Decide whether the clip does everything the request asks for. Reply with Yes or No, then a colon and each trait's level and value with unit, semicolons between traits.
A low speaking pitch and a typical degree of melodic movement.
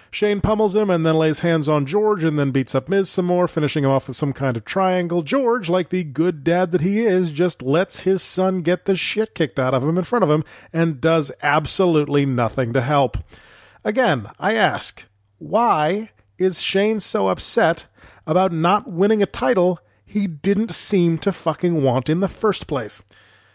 No: medium, 170 Hz; average, 4.9 semitones